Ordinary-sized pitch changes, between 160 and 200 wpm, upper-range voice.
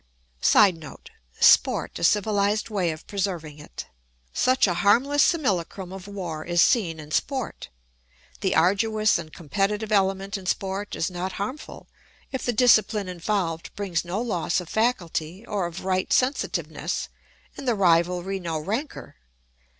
No: average, 3.6 semitones; average, 140 wpm; high, 195 Hz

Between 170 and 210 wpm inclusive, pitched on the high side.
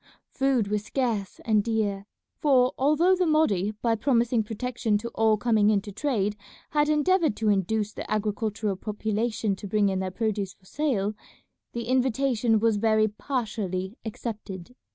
No: average, 155 wpm; high, 220 Hz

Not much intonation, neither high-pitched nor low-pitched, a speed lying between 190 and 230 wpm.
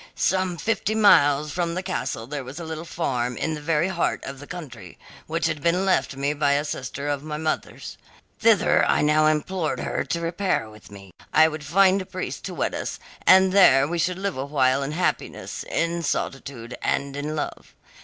No: average, 4.1 semitones; medium, 155 Hz; average, 200 wpm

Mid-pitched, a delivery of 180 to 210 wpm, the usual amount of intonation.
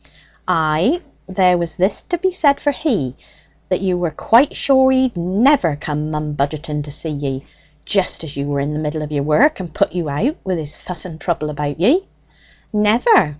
No: medium, 170 Hz; average, 195 wpm; wide, 7.2 semitones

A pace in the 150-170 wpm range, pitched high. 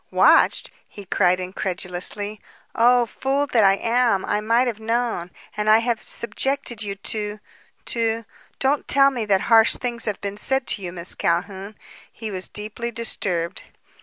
Yes: average, 160 wpm; high, 215 Hz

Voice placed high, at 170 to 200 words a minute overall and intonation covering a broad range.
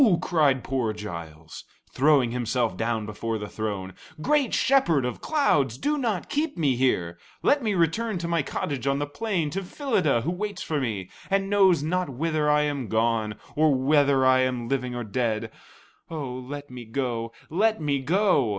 No: medium, 140 Hz; average, 175 wpm; wide, 6.6 semitones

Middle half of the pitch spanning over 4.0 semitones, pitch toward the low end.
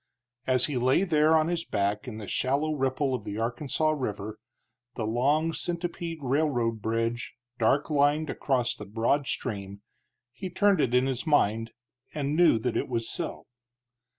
Yes: average, 5.1 semitones; low, 130 Hz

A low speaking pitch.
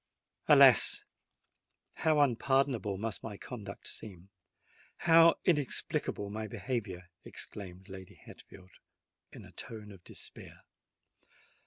Yes: low, 105 Hz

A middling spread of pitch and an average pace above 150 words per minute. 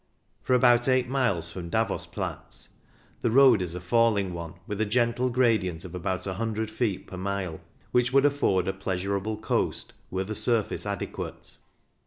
Yes: average, 4.6 semitones; average, 165 wpm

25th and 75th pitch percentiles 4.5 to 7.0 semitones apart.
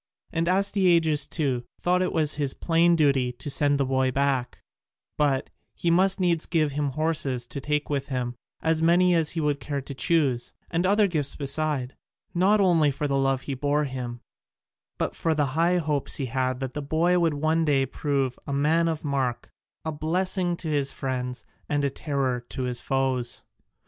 No: average, 3.6 semitones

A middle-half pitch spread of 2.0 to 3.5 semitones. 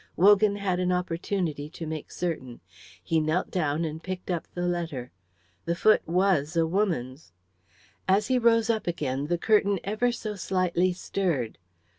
No: average, 3.9 semitones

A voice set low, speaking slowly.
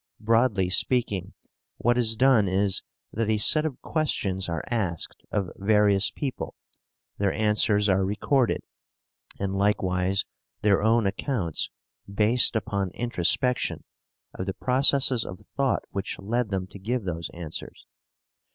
Yes: low, 105 Hz; slow, 130 wpm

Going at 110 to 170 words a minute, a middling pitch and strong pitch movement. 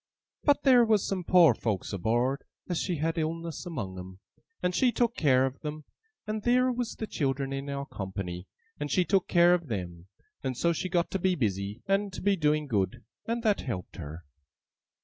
No: average, 190 wpm; medium, 155 Hz; wide, 8.5 semitones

